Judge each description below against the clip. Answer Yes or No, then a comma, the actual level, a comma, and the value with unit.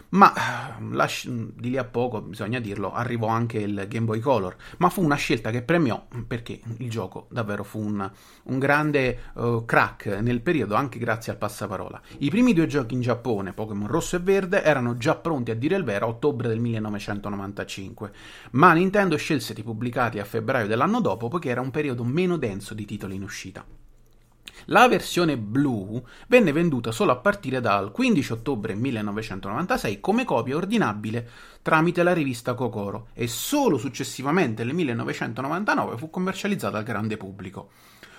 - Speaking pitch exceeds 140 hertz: No, low, 120 Hz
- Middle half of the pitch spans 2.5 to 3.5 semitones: No, wide, 5.6 semitones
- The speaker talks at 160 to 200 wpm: Yes, average, 165 wpm